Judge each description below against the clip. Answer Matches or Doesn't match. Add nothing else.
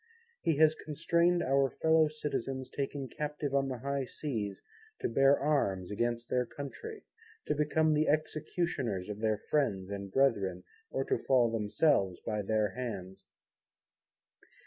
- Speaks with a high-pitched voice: Doesn't match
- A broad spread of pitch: Matches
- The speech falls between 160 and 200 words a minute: Doesn't match